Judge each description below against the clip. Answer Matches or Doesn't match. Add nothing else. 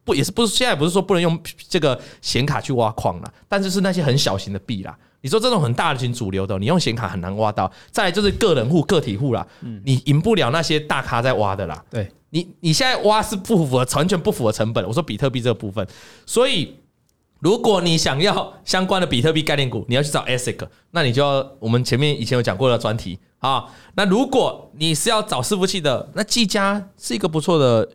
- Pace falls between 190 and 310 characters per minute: Doesn't match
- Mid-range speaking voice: Matches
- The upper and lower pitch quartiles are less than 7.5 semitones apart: Doesn't match